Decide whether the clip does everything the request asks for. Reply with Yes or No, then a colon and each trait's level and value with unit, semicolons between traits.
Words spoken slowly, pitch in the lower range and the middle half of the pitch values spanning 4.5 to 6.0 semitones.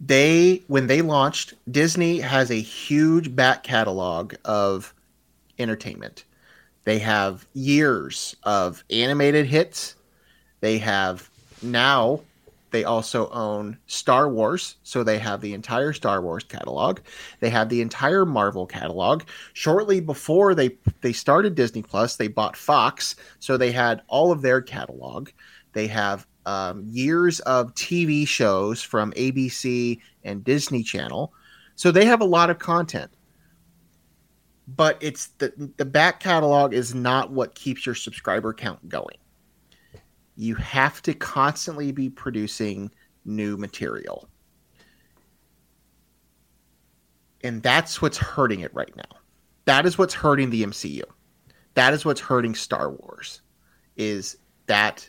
Yes: slow, 130 wpm; low, 125 Hz; wide, 5.4 semitones